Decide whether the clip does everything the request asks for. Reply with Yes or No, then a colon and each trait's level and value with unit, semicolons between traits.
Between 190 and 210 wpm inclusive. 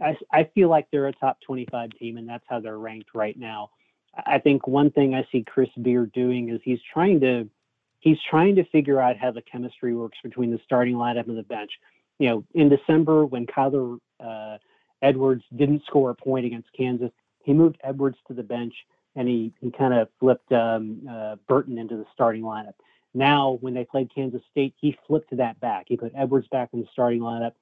Yes: fast, 205 wpm